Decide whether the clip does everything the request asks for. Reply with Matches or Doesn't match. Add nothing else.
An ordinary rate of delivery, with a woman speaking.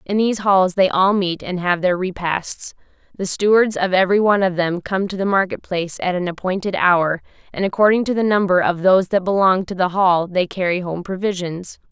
Doesn't match